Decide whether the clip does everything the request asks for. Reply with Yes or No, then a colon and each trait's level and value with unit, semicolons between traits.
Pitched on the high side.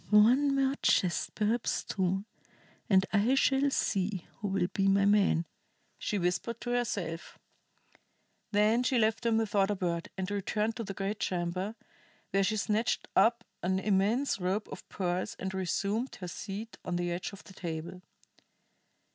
Yes: high, 200 Hz